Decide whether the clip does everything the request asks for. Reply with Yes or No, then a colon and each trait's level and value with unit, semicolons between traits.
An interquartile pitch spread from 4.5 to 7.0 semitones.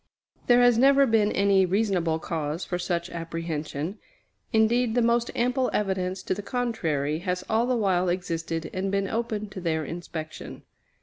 Yes: average, 5.2 semitones